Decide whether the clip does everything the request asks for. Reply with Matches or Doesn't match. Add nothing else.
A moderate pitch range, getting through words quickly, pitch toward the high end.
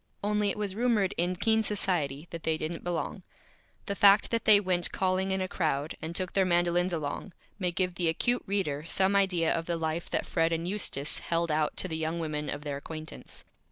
Doesn't match